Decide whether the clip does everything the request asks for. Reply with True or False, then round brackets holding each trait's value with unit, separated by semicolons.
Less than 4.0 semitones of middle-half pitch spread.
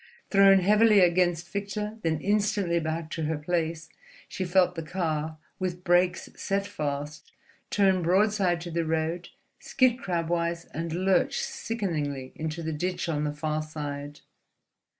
True (3.3 semitones)